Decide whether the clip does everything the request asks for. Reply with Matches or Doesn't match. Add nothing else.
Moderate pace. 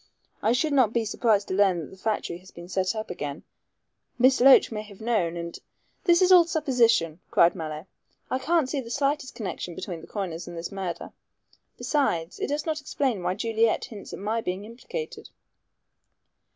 Matches